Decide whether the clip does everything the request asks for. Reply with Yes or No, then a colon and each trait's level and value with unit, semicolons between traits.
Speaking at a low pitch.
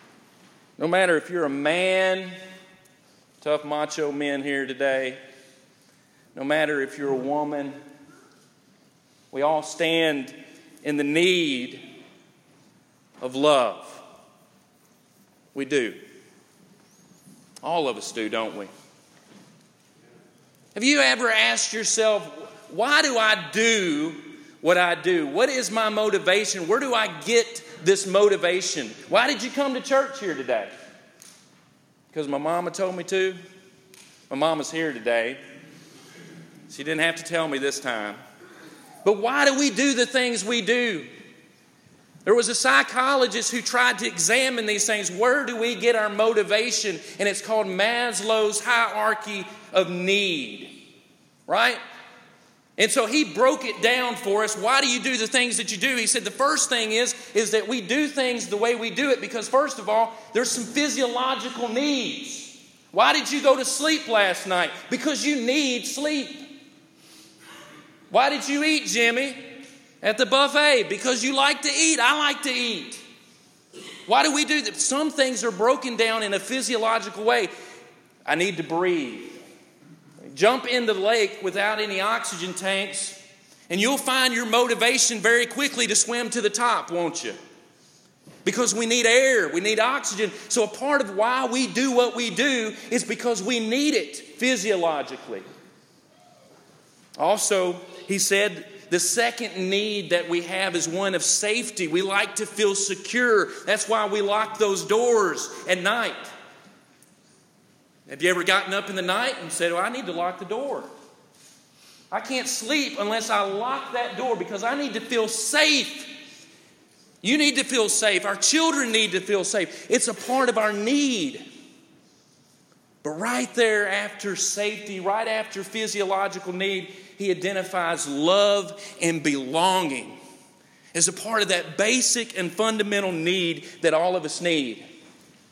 No: high, 215 Hz